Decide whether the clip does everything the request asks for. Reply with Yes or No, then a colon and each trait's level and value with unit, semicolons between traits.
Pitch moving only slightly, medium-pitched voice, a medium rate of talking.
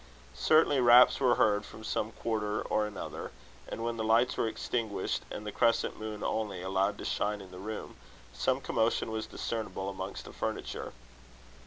No: narrow, 2.0 semitones; low, 110 Hz; average, 170 wpm